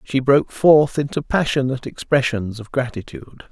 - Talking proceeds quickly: No, slow, 135 wpm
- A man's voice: Yes, male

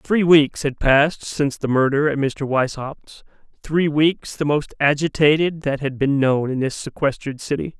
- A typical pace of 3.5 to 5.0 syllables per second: Yes, 4.7 syllables/s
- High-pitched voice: No, medium, 145 Hz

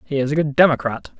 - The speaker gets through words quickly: Yes, fast, 250 wpm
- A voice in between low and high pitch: Yes, medium, 145 Hz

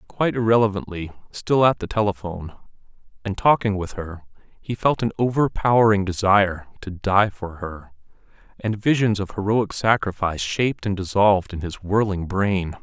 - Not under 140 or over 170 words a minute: Yes, average, 145 wpm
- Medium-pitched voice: No, low, 100 Hz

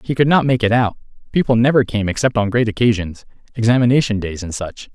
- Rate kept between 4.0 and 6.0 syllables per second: No, 6.2 syllables/s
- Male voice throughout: Yes, male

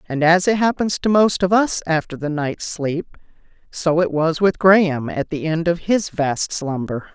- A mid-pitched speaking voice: Yes, medium, 170 Hz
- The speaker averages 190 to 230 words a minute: Yes, average, 200 wpm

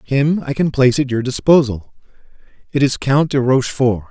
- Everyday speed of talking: Yes, average, 175 wpm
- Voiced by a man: Yes, male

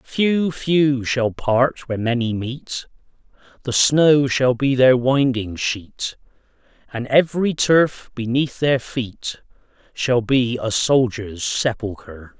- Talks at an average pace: No, slow, 120 wpm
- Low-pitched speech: Yes, low, 125 Hz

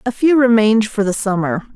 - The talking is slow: No, fast, 205 wpm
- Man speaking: No, female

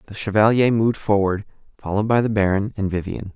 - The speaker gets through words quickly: No, average, 180 wpm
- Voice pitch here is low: Yes, low, 105 Hz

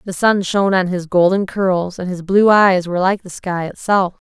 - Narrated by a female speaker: Yes, female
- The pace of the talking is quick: Yes, fast, 225 wpm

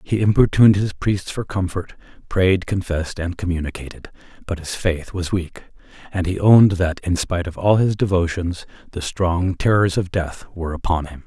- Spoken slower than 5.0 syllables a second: No, 5.2 syllables/s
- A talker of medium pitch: No, very low, 90 Hz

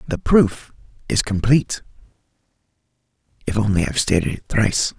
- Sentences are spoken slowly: Yes, slow, 120 wpm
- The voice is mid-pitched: No, low, 110 Hz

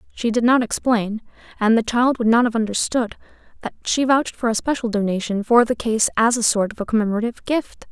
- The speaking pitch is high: Yes, high, 230 Hz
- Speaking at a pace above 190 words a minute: Yes, fast, 205 wpm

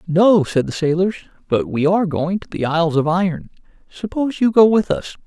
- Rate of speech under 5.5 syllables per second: No, 5.8 syllables/s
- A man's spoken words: Yes, male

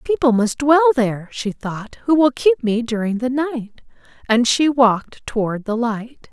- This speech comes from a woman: Yes, female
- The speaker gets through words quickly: No, average, 180 wpm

